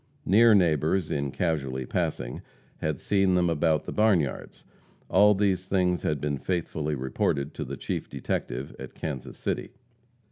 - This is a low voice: Yes, very low, 80 Hz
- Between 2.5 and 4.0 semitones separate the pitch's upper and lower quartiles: No, average, 5.1 semitones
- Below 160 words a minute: Yes, average, 145 wpm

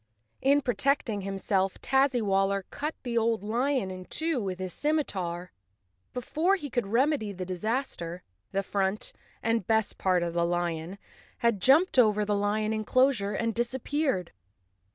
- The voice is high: Yes, high, 215 Hz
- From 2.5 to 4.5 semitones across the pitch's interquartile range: No, wide, 5.5 semitones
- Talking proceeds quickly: No, average, 145 wpm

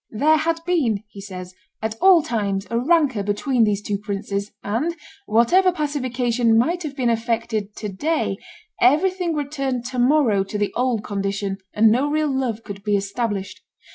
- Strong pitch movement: Yes, wide, 6.0 semitones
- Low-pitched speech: No, high, 235 Hz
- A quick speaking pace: No, average, 165 wpm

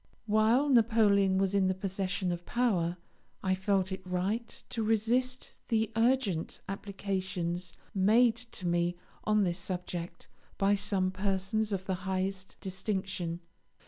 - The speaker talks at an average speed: No, slow, 130 wpm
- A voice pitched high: Yes, high, 195 Hz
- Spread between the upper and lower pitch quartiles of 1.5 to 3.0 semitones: Yes, average, 2.7 semitones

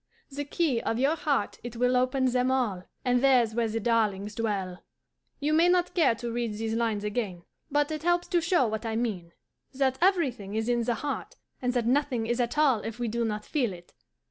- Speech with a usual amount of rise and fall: Yes, average, 3.7 semitones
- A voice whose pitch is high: Yes, high, 240 Hz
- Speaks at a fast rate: Yes, fast, 215 wpm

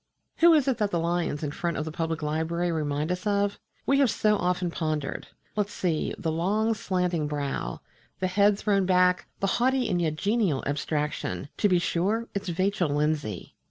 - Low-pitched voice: No, medium, 180 Hz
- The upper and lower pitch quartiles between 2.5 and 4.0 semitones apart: No, average, 4.6 semitones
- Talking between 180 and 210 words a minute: Yes, average, 185 wpm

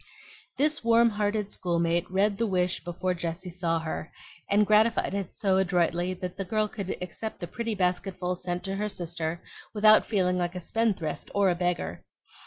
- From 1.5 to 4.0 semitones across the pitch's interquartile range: Yes, average, 3.1 semitones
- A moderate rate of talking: Yes, average, 175 wpm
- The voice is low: No, medium, 185 Hz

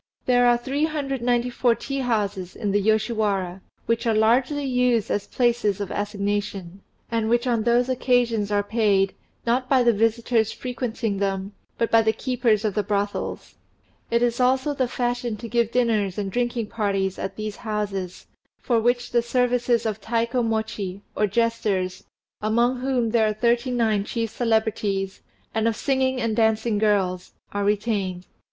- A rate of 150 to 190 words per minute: Yes, average, 155 wpm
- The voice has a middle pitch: No, high, 225 Hz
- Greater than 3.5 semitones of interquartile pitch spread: No, average, 2.9 semitones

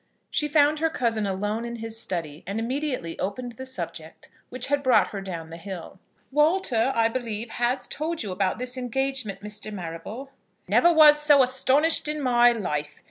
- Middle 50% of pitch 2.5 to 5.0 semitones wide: No, wide, 5.5 semitones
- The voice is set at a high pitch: Yes, high, 235 Hz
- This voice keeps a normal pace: Yes, average, 175 wpm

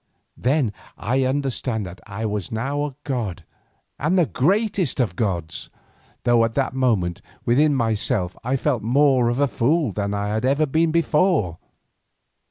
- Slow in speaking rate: No, average, 155 wpm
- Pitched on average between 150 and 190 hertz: No, low, 125 Hz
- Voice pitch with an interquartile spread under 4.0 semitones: No, average, 5.2 semitones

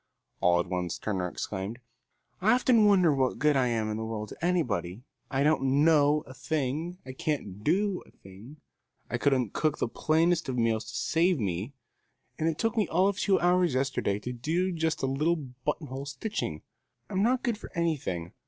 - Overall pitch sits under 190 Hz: Yes, medium, 140 Hz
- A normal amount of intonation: No, wide, 6.8 semitones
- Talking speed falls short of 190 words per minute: No, average, 195 wpm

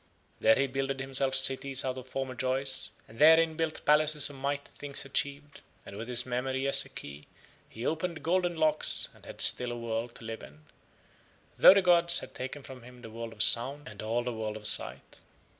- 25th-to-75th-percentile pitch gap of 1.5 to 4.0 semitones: Yes, average, 3.5 semitones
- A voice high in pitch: No, low, 130 Hz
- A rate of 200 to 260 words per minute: Yes, fast, 205 wpm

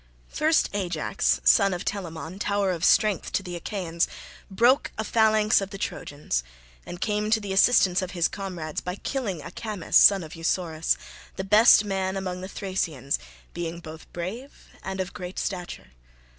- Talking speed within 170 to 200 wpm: No, average, 160 wpm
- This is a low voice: No, high, 190 Hz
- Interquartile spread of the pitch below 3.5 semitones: Yes, average, 3.1 semitones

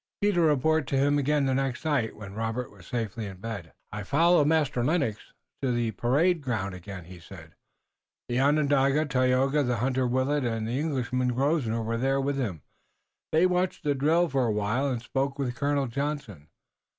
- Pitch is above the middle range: No, low, 130 Hz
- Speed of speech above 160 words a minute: Yes, average, 175 wpm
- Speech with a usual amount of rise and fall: Yes, average, 4.1 semitones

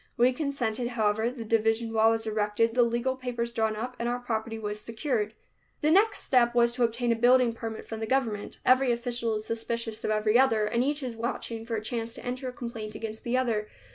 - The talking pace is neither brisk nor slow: No, fast, 220 wpm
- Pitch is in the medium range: No, high, 235 Hz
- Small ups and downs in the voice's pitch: Yes, narrow, 1.9 semitones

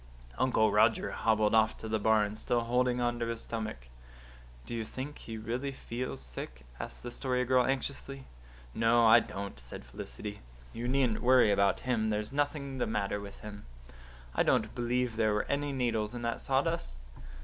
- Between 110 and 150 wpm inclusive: No, average, 175 wpm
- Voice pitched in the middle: No, low, 115 Hz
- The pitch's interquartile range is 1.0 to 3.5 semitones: Yes, average, 2.9 semitones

